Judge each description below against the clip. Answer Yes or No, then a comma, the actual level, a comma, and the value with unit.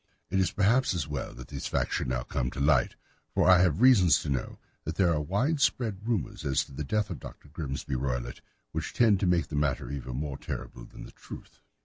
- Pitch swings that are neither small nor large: No, wide, 6.2 semitones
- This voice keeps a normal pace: No, fast, 225 wpm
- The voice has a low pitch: Yes, very low, 75 Hz